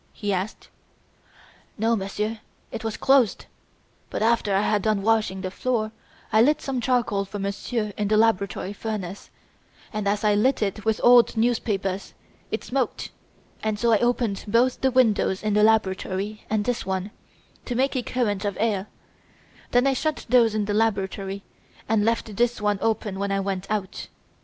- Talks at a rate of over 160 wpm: Yes, average, 170 wpm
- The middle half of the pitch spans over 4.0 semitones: No, average, 2.8 semitones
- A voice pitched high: Yes, high, 215 Hz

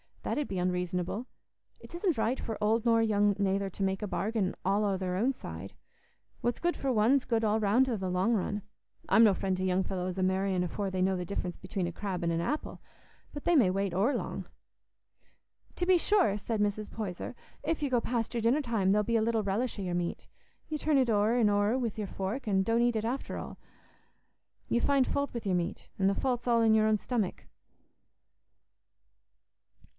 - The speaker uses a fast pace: Yes, fast, 210 wpm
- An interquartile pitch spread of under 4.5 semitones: Yes, average, 3.9 semitones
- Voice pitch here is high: Yes, high, 210 Hz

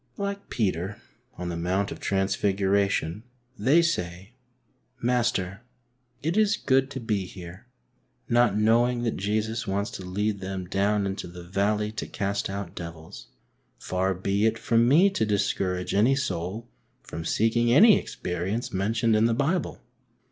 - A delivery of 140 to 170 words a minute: Yes, average, 150 wpm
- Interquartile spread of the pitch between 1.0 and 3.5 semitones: No, average, 3.9 semitones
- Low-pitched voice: Yes, low, 105 Hz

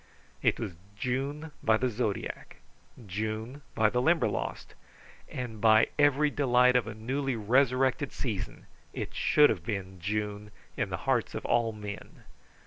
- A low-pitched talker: Yes, low, 115 Hz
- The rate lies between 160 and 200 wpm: No, average, 140 wpm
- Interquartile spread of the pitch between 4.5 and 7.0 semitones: No, average, 3.7 semitones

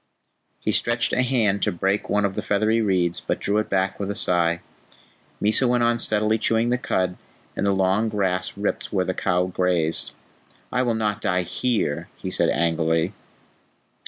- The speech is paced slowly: No, average, 180 wpm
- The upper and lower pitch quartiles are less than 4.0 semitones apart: Yes, average, 3.4 semitones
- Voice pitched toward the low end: Yes, low, 100 Hz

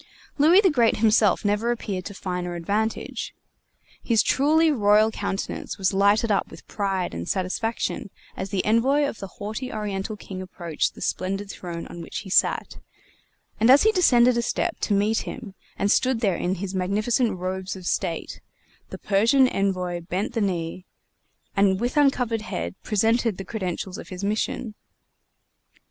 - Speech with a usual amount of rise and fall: Yes, average, 3.7 semitones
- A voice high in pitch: Yes, high, 205 Hz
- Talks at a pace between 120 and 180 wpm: Yes, average, 160 wpm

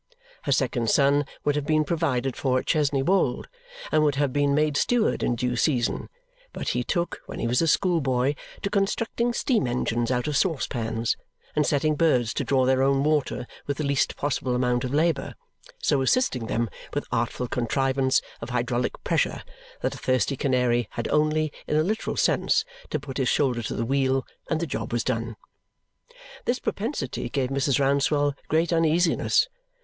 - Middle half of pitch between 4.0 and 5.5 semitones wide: No, average, 3.6 semitones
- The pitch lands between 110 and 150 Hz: Yes, medium, 140 Hz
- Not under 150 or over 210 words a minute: Yes, average, 175 wpm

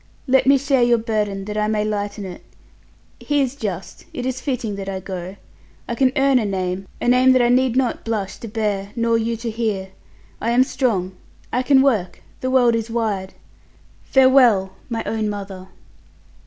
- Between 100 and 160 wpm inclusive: No, average, 185 wpm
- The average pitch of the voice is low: No, high, 225 Hz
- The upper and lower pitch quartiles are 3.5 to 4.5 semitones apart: Yes, average, 4.2 semitones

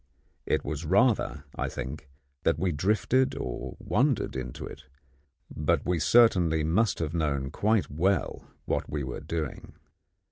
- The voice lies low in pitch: Yes, very low, 80 Hz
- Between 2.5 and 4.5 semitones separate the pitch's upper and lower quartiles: No, average, 5.0 semitones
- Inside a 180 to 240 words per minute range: No, average, 140 wpm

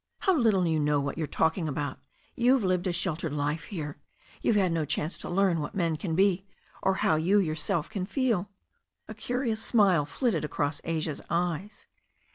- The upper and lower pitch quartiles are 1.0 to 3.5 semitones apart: No, average, 4.4 semitones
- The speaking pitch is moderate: Yes, medium, 175 Hz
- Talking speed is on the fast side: No, average, 185 wpm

